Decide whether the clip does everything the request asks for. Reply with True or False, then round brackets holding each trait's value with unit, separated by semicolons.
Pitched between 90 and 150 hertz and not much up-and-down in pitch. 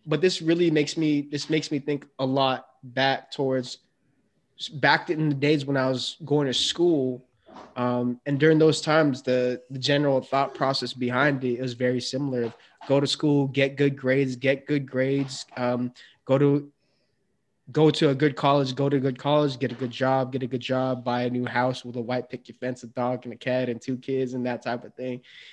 True (135 Hz; 2.3 semitones)